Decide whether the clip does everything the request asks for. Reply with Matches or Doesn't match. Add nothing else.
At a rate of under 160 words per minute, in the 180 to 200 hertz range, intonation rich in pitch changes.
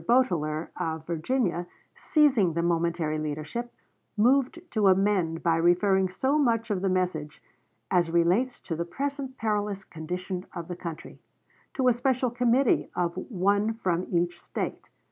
Matches